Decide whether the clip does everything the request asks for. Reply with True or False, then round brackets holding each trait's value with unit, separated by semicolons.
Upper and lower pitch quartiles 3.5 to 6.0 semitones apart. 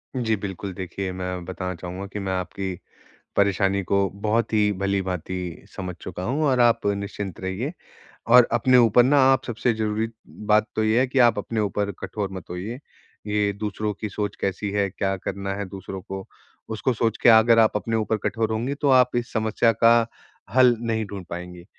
False (2.9 semitones)